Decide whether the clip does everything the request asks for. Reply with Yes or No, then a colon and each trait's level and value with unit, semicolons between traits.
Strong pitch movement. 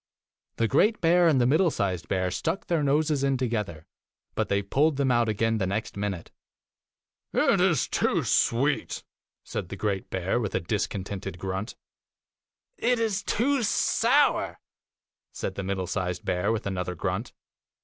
Yes: wide, 7.5 semitones